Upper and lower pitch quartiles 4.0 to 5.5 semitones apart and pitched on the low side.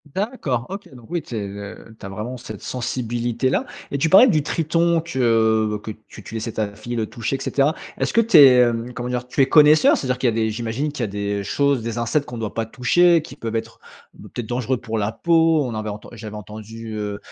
Yes: average, 4.3 semitones; low, 120 Hz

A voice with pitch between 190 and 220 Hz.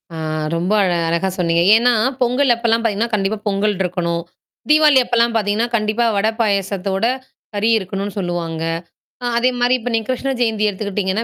Yes: high, 210 Hz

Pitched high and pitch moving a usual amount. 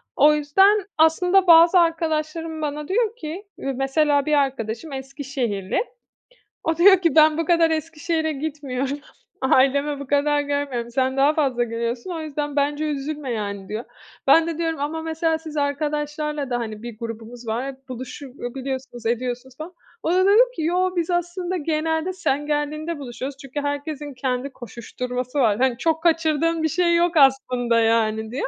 Yes: very high, 290 Hz; average, 3.9 semitones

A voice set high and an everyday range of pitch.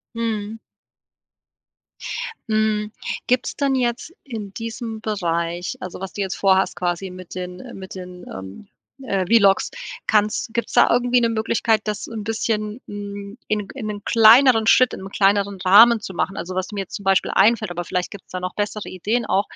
Yes: high, 205 Hz; average, 3.0 semitones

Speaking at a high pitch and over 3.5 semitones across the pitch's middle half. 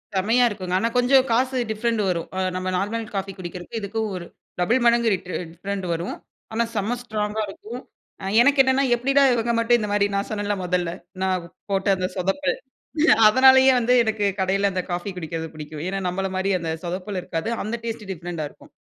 Yes: high, 205 Hz; average, 4.2 semitones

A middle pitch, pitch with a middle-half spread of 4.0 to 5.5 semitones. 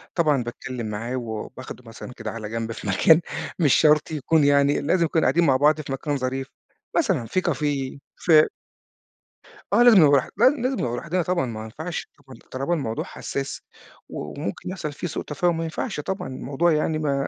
Yes: medium, 145 Hz; average, 4.3 semitones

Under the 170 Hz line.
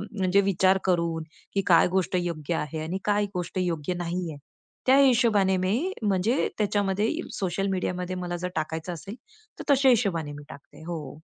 No: medium, 185 Hz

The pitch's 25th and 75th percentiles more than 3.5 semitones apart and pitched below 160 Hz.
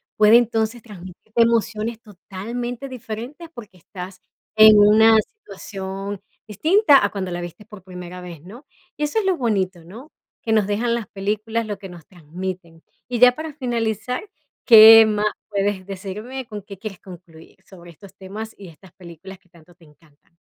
No: average, 3.9 semitones; high, 210 Hz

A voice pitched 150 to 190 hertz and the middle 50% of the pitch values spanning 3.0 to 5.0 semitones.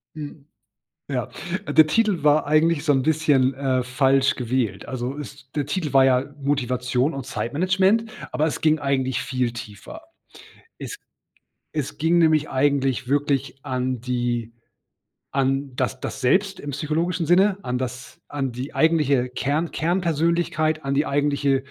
No: medium, 140 Hz; average, 3.3 semitones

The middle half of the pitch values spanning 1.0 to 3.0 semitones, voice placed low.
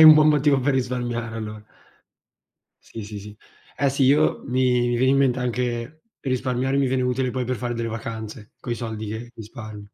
Yes: narrow, 2.6 semitones; low, 125 Hz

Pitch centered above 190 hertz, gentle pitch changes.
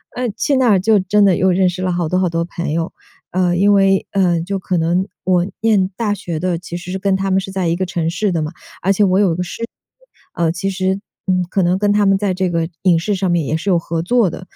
No: medium, 185 Hz; narrow, 2.1 semitones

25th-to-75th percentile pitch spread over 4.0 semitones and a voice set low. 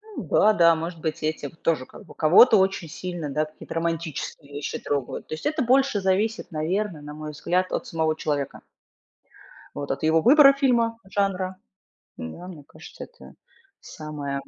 No: average, 4.4 semitones; medium, 165 Hz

